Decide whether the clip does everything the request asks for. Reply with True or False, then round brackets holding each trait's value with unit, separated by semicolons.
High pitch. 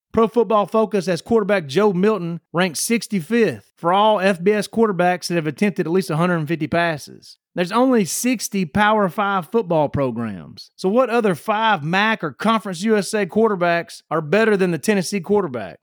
True (200 Hz)